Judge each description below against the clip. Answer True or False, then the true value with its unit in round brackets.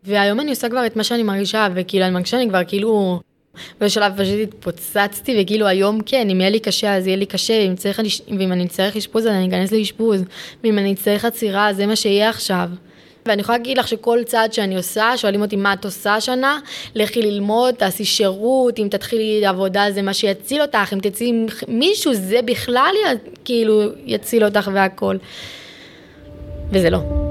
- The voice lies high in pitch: True (210 Hz)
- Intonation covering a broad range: False (2.5 semitones)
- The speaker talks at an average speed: False (180 wpm)